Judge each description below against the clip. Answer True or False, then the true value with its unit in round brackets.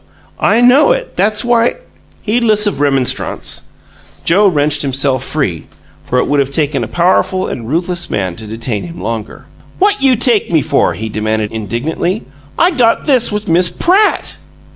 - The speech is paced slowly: False (165 wpm)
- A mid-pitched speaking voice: True (165 Hz)